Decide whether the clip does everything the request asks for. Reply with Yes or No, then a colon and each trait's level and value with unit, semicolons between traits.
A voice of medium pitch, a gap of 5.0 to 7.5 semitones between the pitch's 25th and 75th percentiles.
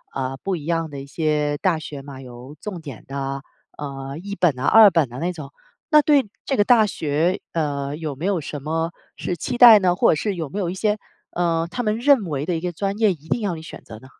Yes: medium, 165 Hz; wide, 5.6 semitones